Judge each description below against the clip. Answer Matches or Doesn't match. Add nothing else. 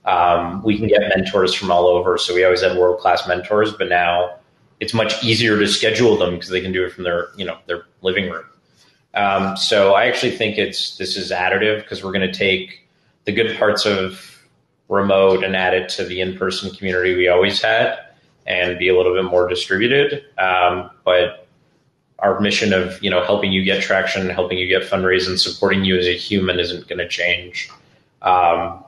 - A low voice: Matches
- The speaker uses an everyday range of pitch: Doesn't match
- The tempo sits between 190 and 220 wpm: Matches